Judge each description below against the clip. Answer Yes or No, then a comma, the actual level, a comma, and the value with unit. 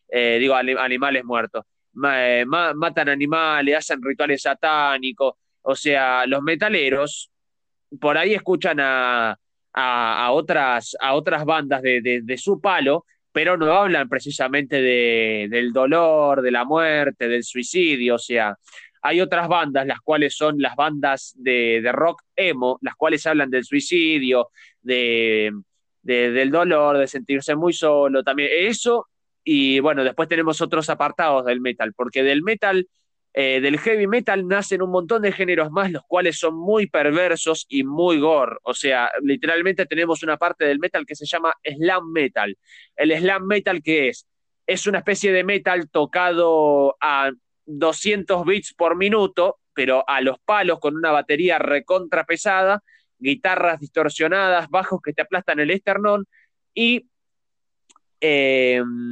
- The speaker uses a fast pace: No, average, 150 wpm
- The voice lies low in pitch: No, medium, 155 Hz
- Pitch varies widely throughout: No, average, 5.0 semitones